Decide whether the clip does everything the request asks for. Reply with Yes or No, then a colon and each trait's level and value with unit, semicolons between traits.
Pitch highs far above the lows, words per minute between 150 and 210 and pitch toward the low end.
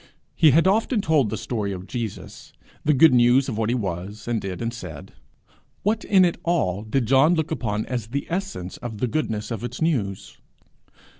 Yes: wide, 7.0 semitones; average, 195 wpm; low, 120 Hz